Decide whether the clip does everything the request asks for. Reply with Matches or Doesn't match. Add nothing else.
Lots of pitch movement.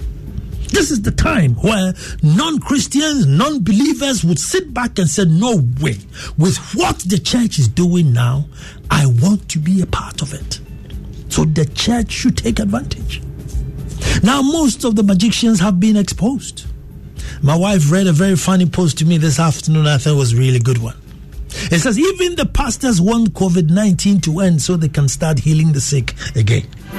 Matches